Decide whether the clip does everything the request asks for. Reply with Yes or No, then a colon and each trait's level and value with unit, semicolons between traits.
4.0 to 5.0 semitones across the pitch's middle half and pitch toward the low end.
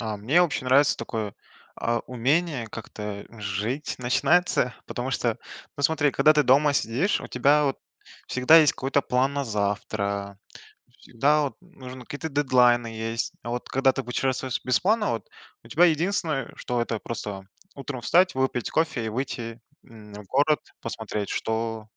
Yes: average, 4.3 semitones; low, 125 Hz